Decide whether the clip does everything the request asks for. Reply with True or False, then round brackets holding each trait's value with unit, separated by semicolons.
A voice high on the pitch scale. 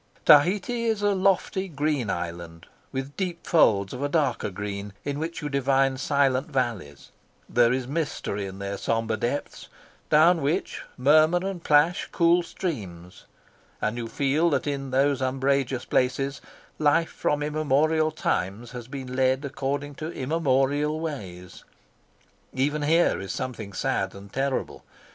False (140 Hz)